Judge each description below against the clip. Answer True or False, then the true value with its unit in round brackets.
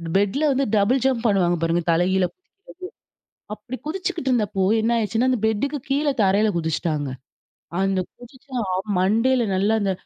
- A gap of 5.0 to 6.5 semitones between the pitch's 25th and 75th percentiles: True (5.3 semitones)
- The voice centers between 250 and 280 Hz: False (220 Hz)